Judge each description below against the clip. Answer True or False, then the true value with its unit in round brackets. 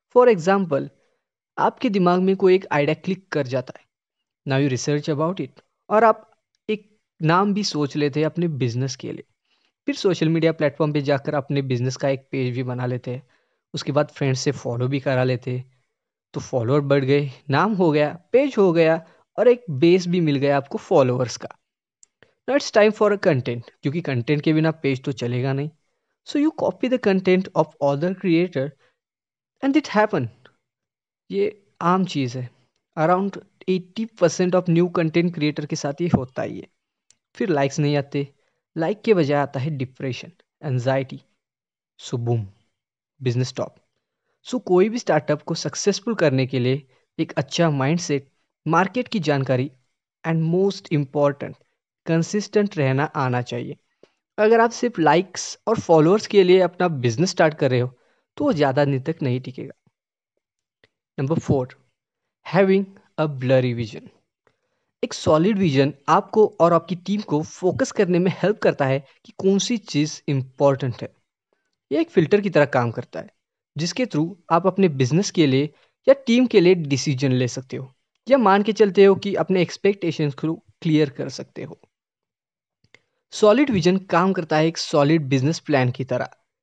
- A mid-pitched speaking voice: True (155 Hz)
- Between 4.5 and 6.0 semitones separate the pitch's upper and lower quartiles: True (5.6 semitones)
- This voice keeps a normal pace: True (170 wpm)